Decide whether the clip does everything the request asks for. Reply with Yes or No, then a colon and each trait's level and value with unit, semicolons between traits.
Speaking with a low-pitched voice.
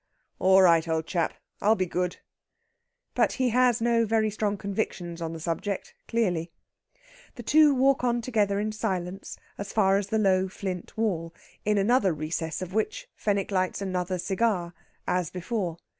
No: high, 195 Hz